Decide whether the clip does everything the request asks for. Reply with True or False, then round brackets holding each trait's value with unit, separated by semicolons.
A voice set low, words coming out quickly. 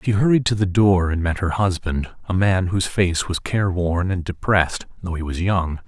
True (90 Hz; 215 wpm)